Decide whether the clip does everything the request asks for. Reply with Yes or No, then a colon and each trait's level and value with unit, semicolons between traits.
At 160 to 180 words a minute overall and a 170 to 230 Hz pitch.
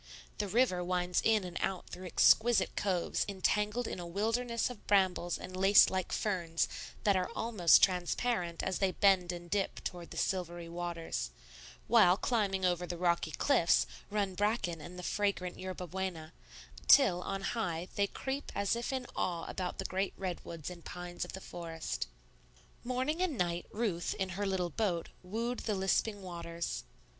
Yes: average, 165 wpm; medium, 185 Hz